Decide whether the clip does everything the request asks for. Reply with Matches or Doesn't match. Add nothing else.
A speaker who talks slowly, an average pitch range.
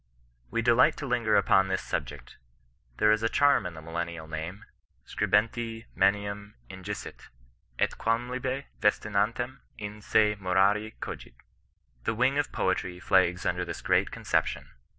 Matches